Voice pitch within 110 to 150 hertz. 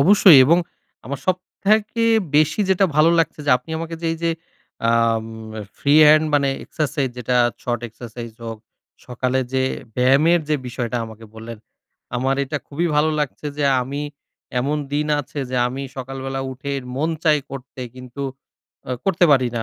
Yes: medium, 140 Hz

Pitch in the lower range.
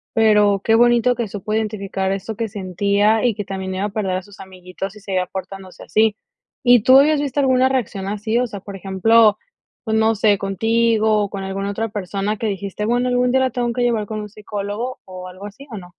No: high, 210 Hz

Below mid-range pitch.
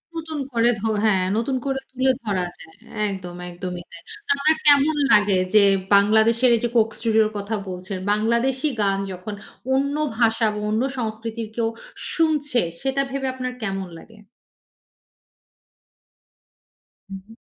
No: high, 225 Hz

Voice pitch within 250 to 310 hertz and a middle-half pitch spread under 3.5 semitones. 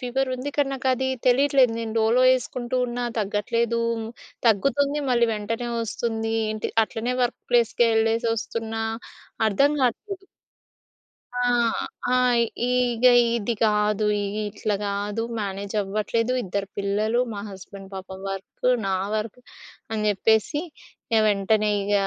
No: high, 225 Hz; average, 3.0 semitones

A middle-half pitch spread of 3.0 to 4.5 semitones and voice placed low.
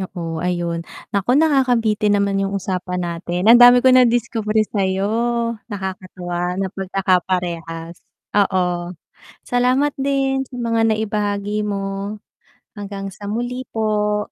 No: average, 3.8 semitones; high, 205 Hz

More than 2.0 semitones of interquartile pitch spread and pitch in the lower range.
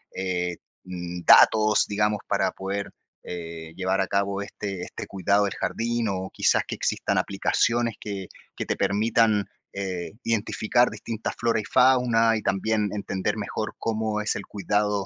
Yes: narrow, 2.6 semitones; low, 105 Hz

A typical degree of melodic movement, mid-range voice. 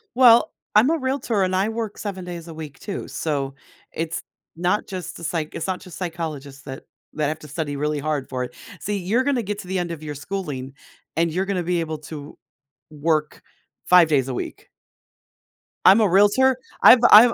Yes: average, 5.0 semitones; medium, 170 Hz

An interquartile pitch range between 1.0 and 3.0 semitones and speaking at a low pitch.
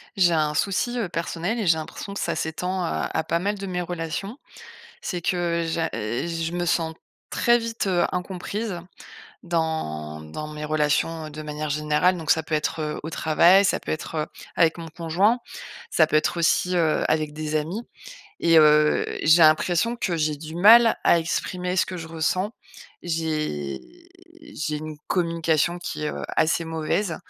No: average, 2.7 semitones; medium, 165 Hz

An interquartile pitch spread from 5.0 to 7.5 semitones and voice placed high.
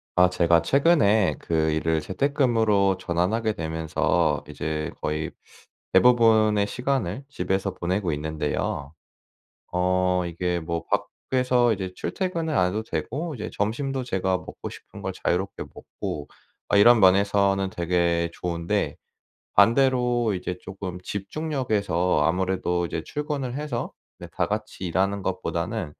No: wide, 5.4 semitones; very low, 95 Hz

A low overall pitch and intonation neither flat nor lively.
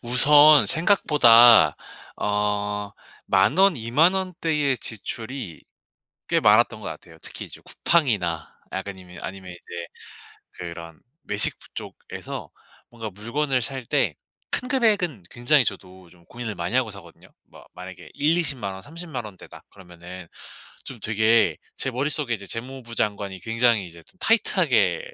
No: low, 115 Hz; wide, 7.1 semitones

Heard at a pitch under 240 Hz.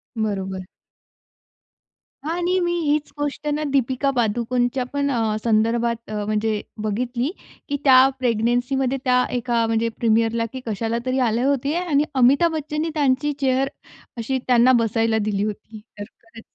No: high, 245 Hz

